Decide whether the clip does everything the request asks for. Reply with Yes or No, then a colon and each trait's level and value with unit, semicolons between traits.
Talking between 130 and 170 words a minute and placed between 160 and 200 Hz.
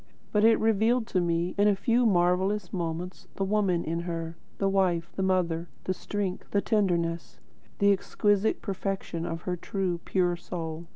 Yes: average, 165 wpm; medium, 185 Hz